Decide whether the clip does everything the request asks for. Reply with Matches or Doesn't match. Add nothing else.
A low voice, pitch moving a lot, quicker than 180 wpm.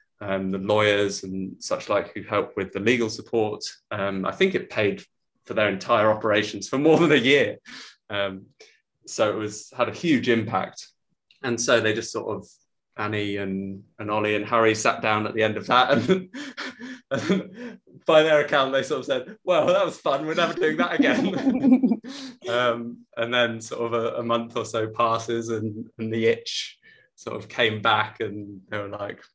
Matches